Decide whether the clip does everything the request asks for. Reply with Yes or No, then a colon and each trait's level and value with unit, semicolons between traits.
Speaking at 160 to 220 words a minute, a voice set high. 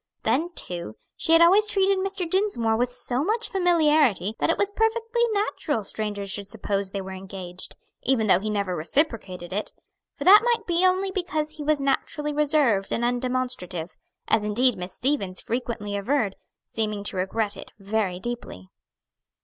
Yes: average, 165 wpm; high, 240 Hz